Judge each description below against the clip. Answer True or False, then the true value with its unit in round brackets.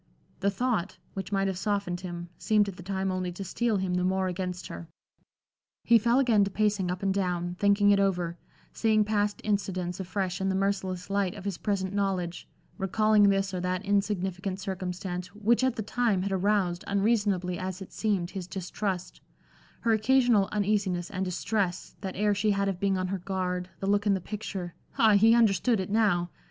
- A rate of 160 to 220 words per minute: True (190 wpm)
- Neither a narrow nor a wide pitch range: False (2.1 semitones)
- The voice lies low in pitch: False (195 Hz)